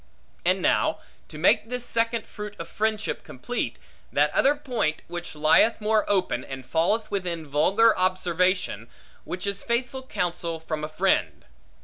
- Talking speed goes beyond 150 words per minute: No, average, 145 wpm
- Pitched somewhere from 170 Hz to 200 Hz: Yes, medium, 185 Hz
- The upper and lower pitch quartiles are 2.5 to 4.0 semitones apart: No, average, 5.3 semitones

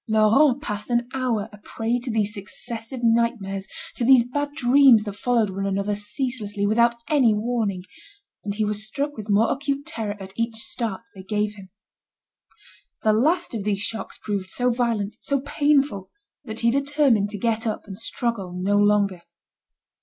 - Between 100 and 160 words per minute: No, average, 170 wpm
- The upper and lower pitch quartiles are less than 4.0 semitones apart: Yes, average, 3.1 semitones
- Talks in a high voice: Yes, high, 225 Hz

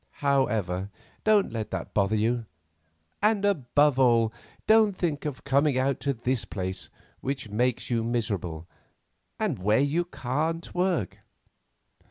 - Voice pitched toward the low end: Yes, low, 130 Hz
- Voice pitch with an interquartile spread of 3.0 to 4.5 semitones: No, wide, 5.4 semitones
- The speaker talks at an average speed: No, slow, 130 wpm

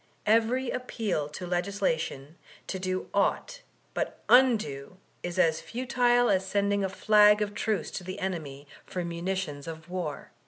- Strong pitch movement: No, average, 4.1 semitones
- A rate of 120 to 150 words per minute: Yes, average, 145 wpm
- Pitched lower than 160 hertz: No, high, 190 Hz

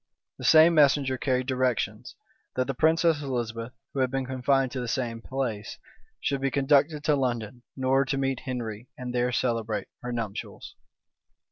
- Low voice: Yes, low, 130 Hz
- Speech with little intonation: Yes, narrow, 2.0 semitones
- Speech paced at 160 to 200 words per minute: Yes, average, 170 wpm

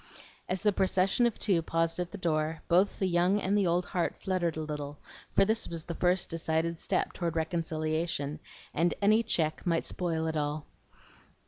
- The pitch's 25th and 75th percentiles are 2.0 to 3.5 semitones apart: Yes, average, 2.8 semitones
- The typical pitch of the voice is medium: Yes, medium, 170 Hz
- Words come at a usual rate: Yes, average, 185 wpm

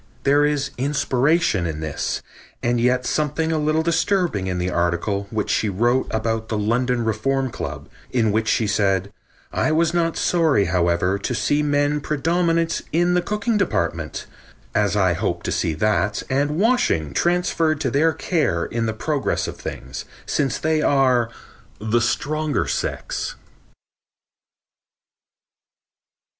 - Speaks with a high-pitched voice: No, low, 130 Hz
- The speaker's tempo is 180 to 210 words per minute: No, average, 140 wpm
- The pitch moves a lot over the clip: Yes, wide, 7.1 semitones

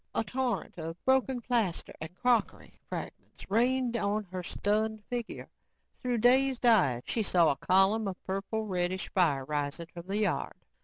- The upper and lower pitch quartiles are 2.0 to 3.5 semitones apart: No, average, 5.1 semitones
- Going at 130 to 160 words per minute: Yes, average, 155 wpm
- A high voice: Yes, high, 210 Hz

